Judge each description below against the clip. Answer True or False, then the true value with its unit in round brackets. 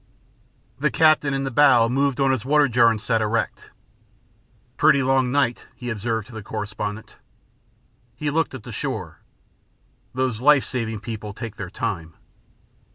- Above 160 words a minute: False (155 wpm)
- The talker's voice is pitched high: False (120 Hz)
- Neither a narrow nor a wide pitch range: True (3.7 semitones)